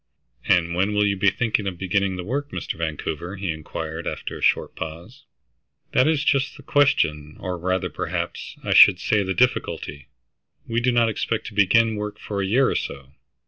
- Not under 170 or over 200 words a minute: Yes, average, 190 wpm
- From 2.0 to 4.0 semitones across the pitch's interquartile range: No, average, 5.0 semitones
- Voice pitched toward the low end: Yes, low, 100 Hz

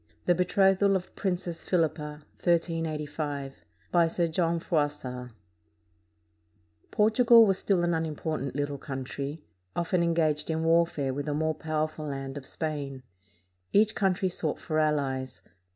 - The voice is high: No, medium, 160 Hz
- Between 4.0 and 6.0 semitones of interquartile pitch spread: No, average, 3.3 semitones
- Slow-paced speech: Yes, slow, 120 wpm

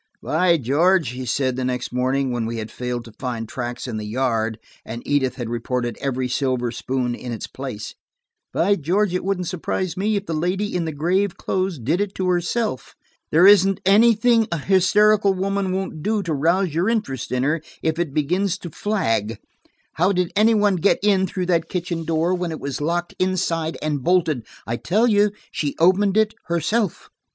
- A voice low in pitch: No, medium, 170 Hz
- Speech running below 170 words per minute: No, average, 190 wpm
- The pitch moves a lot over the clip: Yes, wide, 6.7 semitones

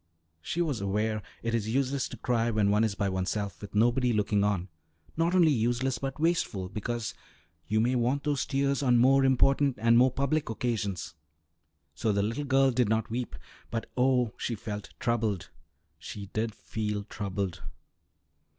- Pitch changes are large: No, average, 4.2 semitones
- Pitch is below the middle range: Yes, low, 115 Hz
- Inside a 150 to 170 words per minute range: Yes, average, 165 wpm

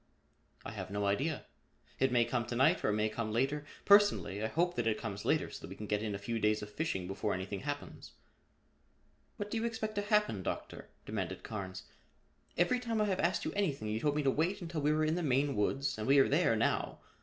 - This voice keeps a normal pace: No, fast, 235 wpm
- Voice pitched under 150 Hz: Yes, low, 135 Hz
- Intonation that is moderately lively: No, wide, 8.1 semitones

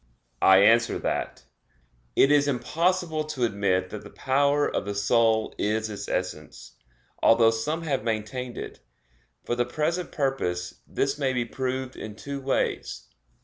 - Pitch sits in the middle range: No, low, 120 Hz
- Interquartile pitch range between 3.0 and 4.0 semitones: No, average, 4.8 semitones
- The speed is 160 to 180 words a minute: No, average, 145 wpm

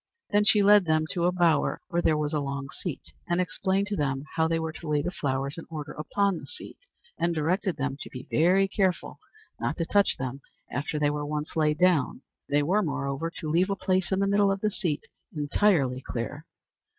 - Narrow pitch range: No, average, 4.4 semitones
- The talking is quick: Yes, fast, 215 wpm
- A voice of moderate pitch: Yes, medium, 160 Hz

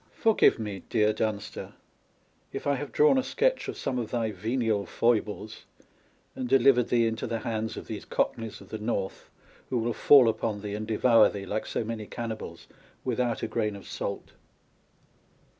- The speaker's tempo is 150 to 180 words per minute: Yes, average, 175 wpm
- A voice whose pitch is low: Yes, low, 115 Hz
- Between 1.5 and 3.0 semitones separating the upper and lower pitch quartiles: Yes, narrow, 2.4 semitones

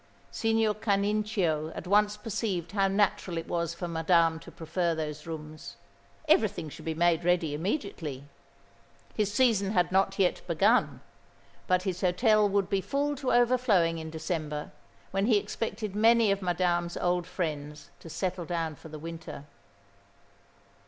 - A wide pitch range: No, average, 4.1 semitones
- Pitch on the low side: No, medium, 180 Hz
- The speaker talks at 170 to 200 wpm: No, average, 145 wpm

